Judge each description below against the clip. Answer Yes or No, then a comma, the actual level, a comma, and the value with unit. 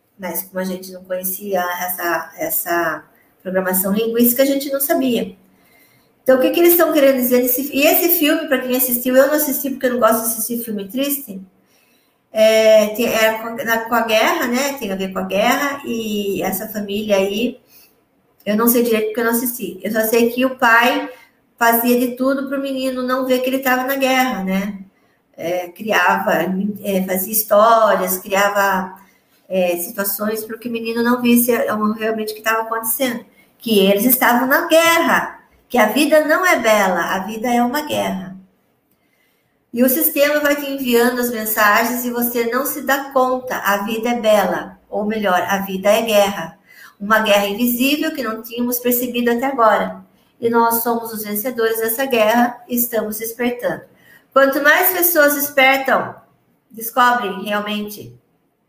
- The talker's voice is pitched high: Yes, high, 230 Hz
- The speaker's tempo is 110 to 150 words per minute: No, average, 175 wpm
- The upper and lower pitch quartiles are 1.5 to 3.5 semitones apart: No, average, 3.9 semitones